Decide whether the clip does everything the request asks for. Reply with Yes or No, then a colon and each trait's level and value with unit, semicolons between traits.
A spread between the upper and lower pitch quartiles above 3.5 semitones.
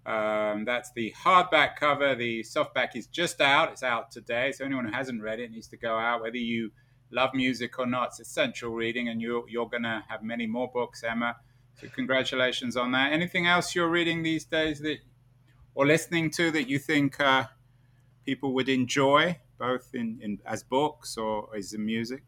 No: average, 3.0 semitones